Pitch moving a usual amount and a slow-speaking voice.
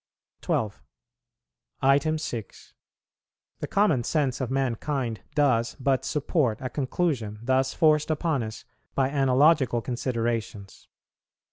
Yes: average, 4.1 semitones; slow, 100 wpm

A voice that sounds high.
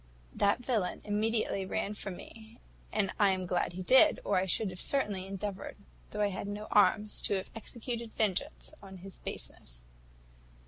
Yes: high, 205 Hz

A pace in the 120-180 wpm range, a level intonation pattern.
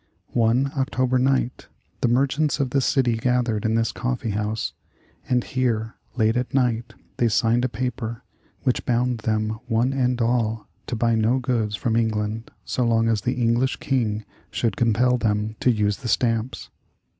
Yes: average, 165 wpm; narrow, 2.2 semitones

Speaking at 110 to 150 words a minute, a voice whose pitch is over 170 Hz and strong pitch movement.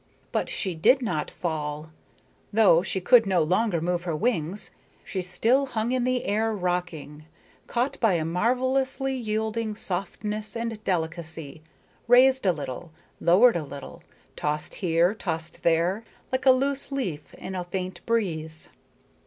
Yes: average, 145 wpm; high, 190 Hz; wide, 5.9 semitones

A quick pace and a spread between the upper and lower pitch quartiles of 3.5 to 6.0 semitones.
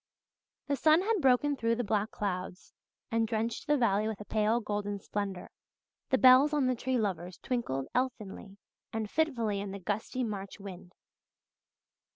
No: average, 160 wpm; average, 4.2 semitones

